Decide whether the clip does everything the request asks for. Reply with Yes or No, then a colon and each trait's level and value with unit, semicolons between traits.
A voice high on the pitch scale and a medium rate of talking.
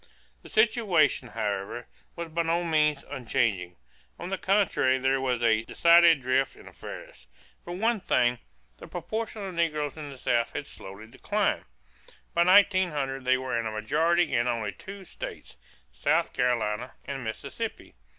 No: low, 135 Hz; average, 150 wpm